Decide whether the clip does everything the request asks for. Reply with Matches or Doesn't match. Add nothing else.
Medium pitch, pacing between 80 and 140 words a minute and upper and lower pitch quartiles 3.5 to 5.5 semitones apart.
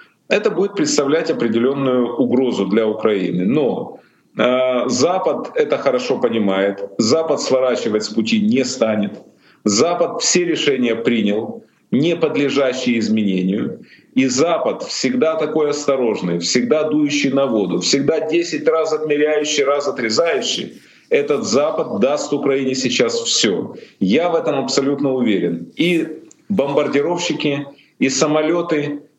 Matches